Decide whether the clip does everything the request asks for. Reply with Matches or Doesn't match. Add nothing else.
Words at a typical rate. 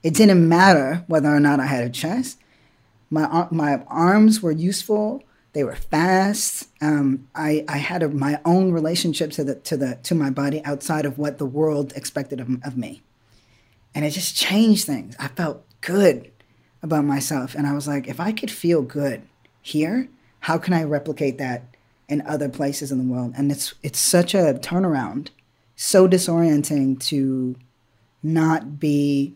Matches